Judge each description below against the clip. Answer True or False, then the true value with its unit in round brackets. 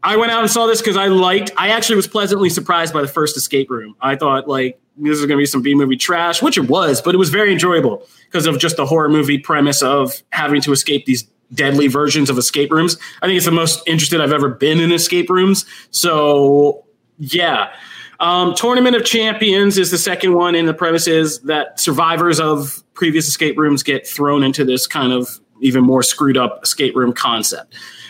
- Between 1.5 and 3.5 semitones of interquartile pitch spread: False (4.2 semitones)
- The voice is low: False (155 Hz)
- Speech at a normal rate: False (215 wpm)